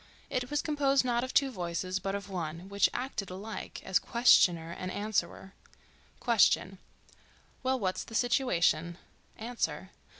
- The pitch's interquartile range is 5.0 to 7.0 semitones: Yes, average, 5.3 semitones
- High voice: Yes, high, 200 Hz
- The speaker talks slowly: Yes, slow, 125 wpm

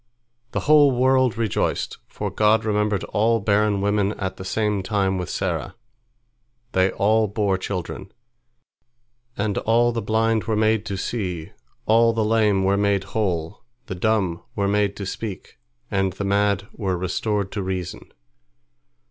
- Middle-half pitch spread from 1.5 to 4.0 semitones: Yes, narrow, 2.4 semitones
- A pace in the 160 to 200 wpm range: No, average, 150 wpm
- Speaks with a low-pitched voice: Yes, low, 105 Hz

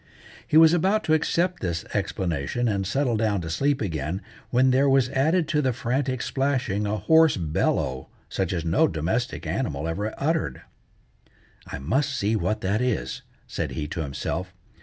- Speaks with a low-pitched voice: Yes, low, 110 Hz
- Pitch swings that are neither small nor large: No, wide, 7.5 semitones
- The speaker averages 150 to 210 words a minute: Yes, average, 165 wpm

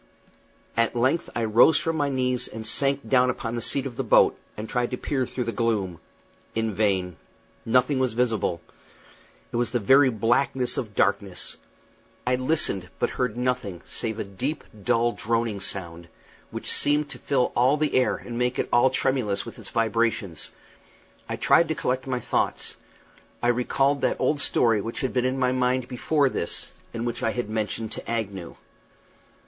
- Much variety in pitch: No, average, 2.7 semitones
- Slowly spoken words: No, average, 175 wpm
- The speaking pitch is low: Yes, low, 120 Hz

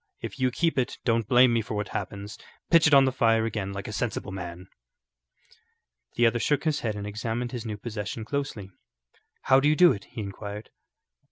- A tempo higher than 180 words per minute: Yes, average, 200 wpm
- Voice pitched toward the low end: Yes, low, 115 Hz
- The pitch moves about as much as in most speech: Yes, average, 3.8 semitones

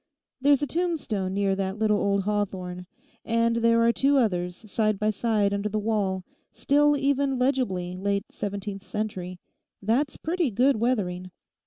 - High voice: Yes, high, 215 Hz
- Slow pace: No, average, 150 wpm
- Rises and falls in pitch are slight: No, average, 4.5 semitones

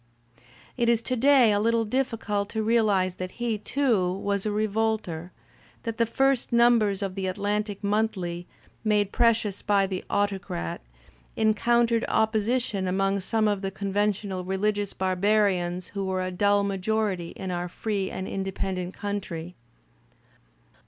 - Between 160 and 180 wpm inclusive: No, average, 145 wpm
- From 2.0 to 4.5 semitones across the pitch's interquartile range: Yes, narrow, 2.6 semitones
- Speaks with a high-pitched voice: Yes, high, 205 Hz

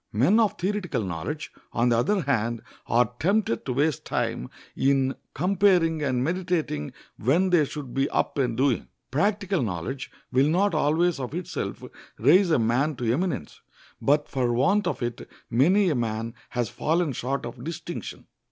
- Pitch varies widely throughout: Yes, wide, 6.5 semitones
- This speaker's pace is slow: No, average, 160 wpm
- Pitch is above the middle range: No, medium, 140 Hz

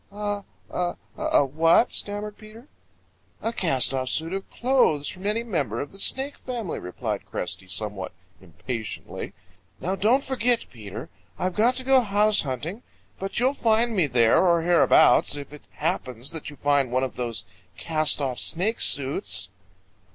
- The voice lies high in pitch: No, medium, 170 Hz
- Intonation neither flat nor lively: No, wide, 8.4 semitones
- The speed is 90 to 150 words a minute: No, average, 160 wpm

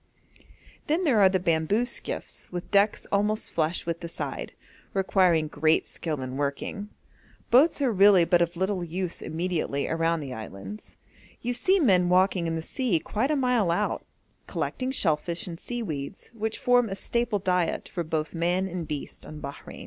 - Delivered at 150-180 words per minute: Yes, average, 170 wpm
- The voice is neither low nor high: Yes, medium, 180 Hz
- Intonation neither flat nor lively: Yes, average, 4.5 semitones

